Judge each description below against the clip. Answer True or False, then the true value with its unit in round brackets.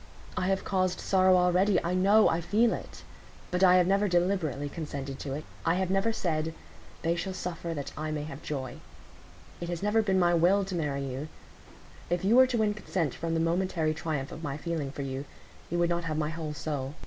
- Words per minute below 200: False (205 wpm)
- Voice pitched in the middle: True (170 Hz)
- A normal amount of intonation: True (3.6 semitones)